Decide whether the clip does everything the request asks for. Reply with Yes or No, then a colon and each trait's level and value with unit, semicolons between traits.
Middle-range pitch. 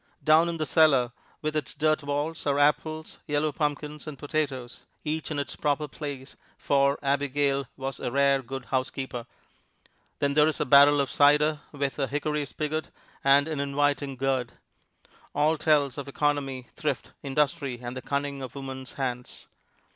Yes: medium, 145 Hz